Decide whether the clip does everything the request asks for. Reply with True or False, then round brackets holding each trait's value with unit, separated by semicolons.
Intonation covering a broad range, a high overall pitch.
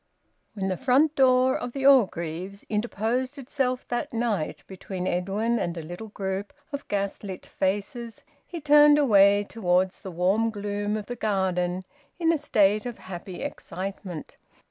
False (4.9 semitones; 205 Hz)